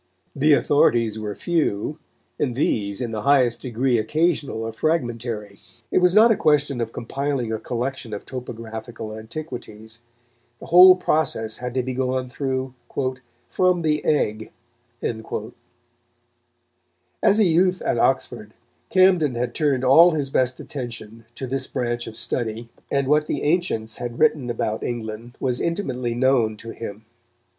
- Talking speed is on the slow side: No, average, 145 wpm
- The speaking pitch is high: No, low, 125 Hz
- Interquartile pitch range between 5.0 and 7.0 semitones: No, average, 4.3 semitones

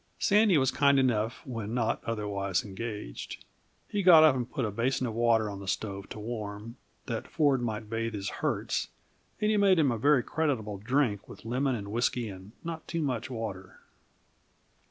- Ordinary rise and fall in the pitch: Yes, average, 4.6 semitones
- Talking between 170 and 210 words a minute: Yes, average, 180 wpm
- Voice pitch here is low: Yes, low, 115 Hz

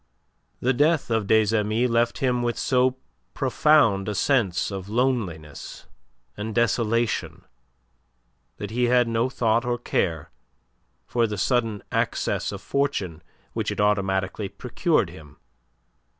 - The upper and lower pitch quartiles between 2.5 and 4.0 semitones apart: Yes, average, 3.7 semitones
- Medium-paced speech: No, slow, 125 wpm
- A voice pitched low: Yes, low, 115 Hz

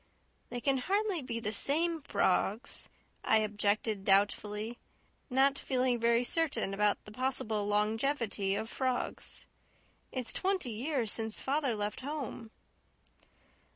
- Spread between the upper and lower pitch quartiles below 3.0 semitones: No, average, 4.6 semitones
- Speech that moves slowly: Yes, slow, 120 wpm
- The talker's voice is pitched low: No, high, 235 Hz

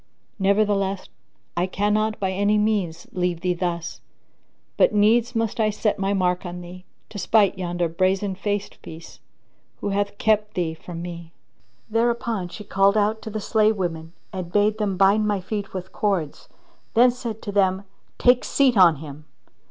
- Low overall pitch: No, high, 195 Hz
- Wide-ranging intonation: No, average, 3.0 semitones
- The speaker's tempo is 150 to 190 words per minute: Yes, average, 170 wpm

